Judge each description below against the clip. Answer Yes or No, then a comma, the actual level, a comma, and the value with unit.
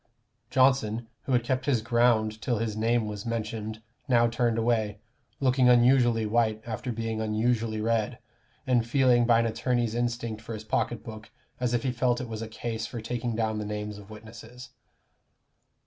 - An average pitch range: No, narrow, 1.8 semitones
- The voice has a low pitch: Yes, low, 115 Hz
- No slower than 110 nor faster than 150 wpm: No, average, 175 wpm